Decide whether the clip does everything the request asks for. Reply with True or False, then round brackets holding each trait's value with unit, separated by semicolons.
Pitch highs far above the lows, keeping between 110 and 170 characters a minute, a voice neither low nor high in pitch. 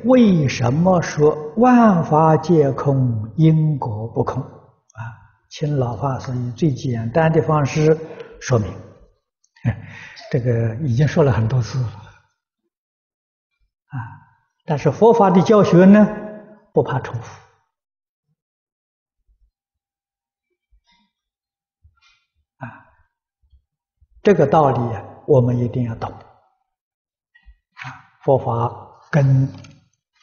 True (7.6 semitones; 125 characters per minute; 150 Hz)